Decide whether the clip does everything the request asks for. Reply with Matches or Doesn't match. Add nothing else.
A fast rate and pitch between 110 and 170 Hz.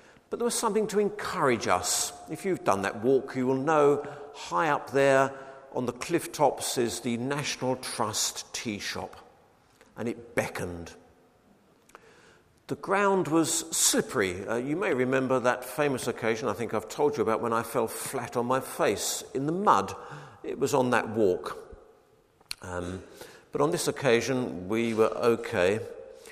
Doesn't match